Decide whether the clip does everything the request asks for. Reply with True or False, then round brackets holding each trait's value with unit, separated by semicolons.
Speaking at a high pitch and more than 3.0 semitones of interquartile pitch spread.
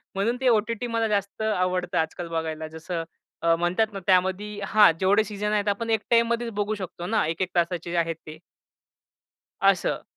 True (195 Hz; 3.8 semitones)